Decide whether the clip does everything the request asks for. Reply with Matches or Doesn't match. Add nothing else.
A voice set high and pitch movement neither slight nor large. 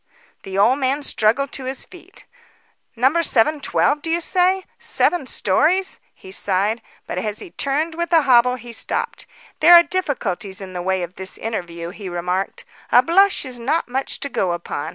Doesn't match